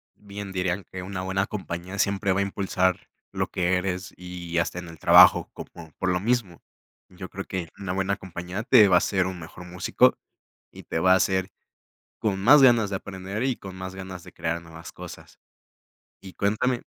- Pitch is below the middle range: Yes, very low, 95 Hz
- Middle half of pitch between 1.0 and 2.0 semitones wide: Yes, narrow, 1.7 semitones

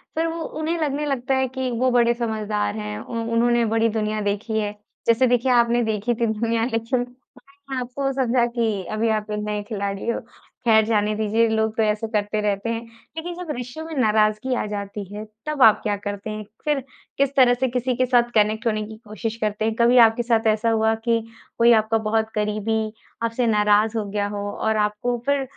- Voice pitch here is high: Yes, high, 225 Hz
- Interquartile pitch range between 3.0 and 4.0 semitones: No, narrow, 2.6 semitones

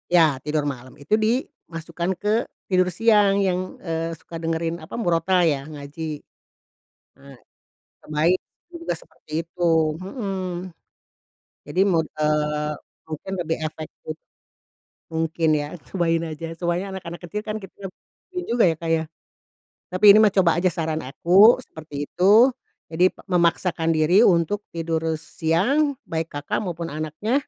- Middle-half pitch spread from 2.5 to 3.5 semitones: Yes, average, 3.2 semitones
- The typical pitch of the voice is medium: Yes, medium, 170 Hz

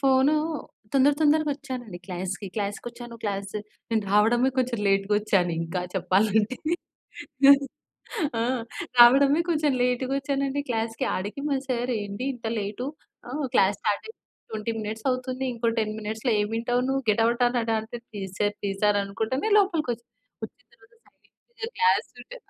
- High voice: Yes, high, 235 Hz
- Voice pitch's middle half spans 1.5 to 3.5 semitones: No, average, 4.3 semitones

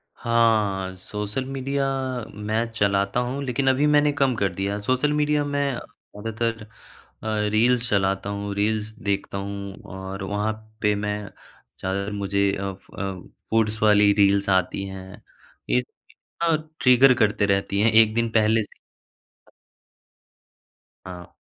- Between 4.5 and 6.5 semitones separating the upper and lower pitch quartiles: No, average, 2.9 semitones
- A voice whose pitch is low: Yes, low, 105 Hz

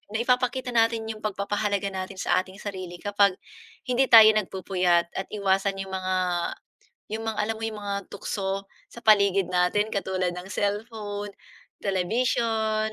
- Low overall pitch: No, high, 205 Hz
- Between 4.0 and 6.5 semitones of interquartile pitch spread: No, narrow, 2.6 semitones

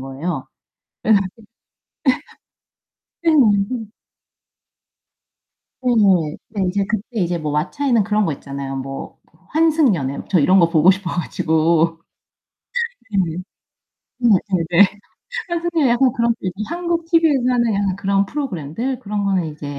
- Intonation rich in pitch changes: Yes, wide, 7.1 semitones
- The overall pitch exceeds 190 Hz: Yes, high, 200 Hz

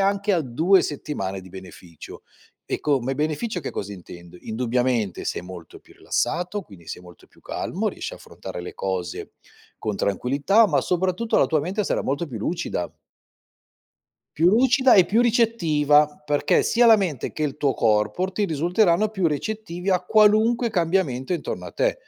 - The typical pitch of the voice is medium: Yes, medium, 155 Hz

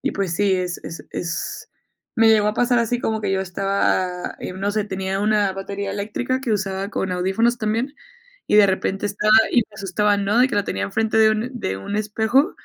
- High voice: Yes, high, 205 Hz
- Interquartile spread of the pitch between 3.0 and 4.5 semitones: No, narrow, 2.4 semitones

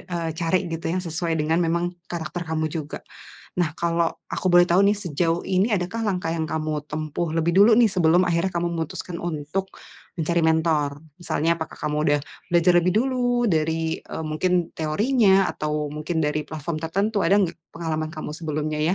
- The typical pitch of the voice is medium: Yes, medium, 165 Hz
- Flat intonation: Yes, narrow, 2.2 semitones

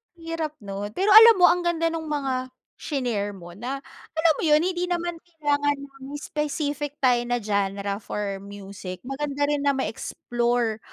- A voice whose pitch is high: Yes, very high, 280 Hz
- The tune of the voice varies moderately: No, wide, 7.1 semitones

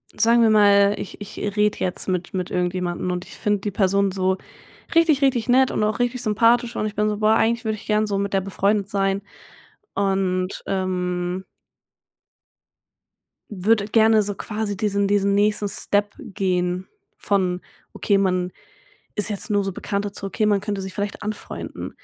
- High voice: Yes, high, 200 Hz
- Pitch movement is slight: Yes, narrow, 2.0 semitones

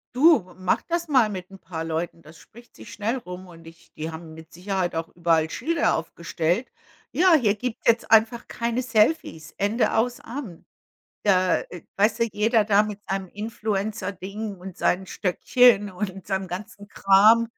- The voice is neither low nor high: No, high, 200 Hz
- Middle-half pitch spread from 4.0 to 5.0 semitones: Yes, average, 4.4 semitones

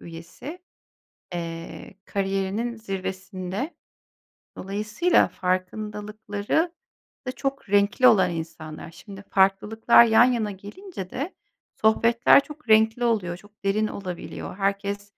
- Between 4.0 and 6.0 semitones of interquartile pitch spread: No, average, 3.3 semitones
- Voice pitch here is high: Yes, high, 205 Hz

